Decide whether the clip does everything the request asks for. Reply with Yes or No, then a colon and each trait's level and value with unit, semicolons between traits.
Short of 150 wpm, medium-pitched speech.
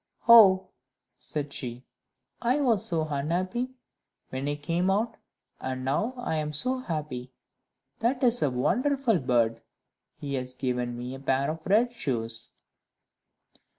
Yes: slow, 135 wpm; medium, 150 Hz